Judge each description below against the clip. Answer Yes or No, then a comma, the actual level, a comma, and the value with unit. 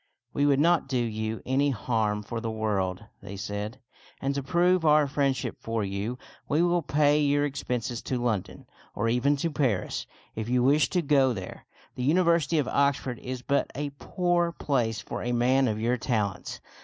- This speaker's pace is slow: No, average, 185 wpm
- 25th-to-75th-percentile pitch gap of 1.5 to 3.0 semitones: No, average, 4.5 semitones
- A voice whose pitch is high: No, low, 130 Hz